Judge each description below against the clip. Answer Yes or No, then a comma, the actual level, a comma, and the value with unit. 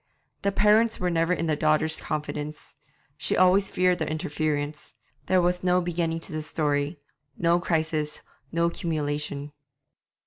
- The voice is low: No, medium, 165 Hz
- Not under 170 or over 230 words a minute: No, average, 140 wpm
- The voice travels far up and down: No, average, 2.8 semitones